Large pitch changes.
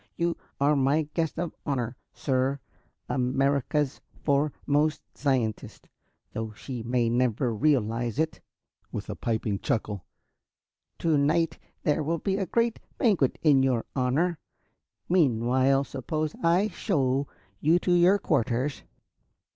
No: average, 4.3 semitones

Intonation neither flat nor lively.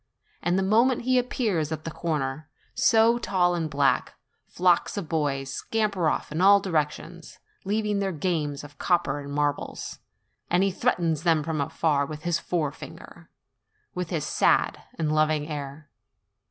Yes: average, 4.3 semitones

